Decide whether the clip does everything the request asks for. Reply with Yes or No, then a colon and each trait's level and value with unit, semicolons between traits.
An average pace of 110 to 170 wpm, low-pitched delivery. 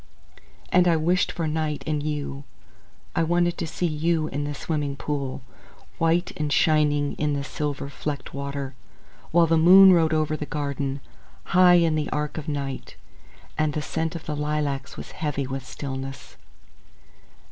No: average, 160 wpm; medium, 150 Hz